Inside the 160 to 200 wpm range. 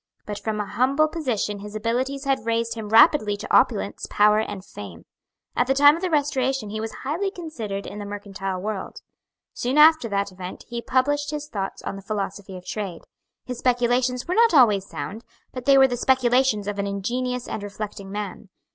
Yes: average, 190 wpm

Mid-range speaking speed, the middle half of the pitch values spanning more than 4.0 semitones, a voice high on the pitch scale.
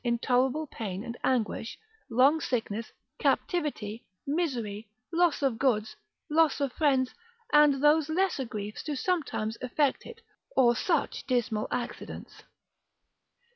No: slow, 115 wpm; average, 4.7 semitones; very high, 260 Hz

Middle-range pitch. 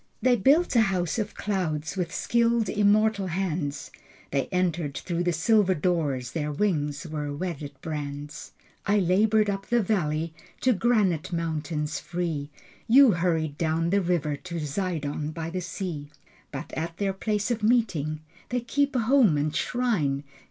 Yes: medium, 175 Hz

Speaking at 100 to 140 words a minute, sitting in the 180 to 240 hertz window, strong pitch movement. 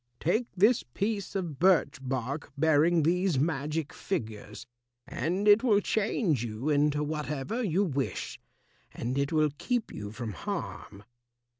No: slow, 135 wpm; medium, 155 Hz; wide, 6.2 semitones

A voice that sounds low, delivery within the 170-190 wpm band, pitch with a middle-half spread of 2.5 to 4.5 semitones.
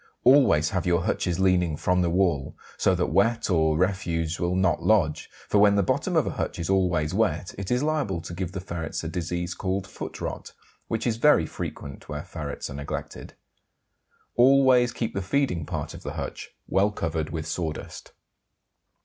Yes: very low, 90 Hz; average, 185 wpm; average, 3.8 semitones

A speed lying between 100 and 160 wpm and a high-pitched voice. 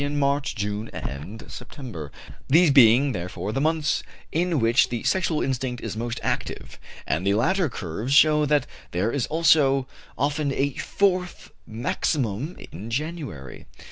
No: average, 140 wpm; low, 135 Hz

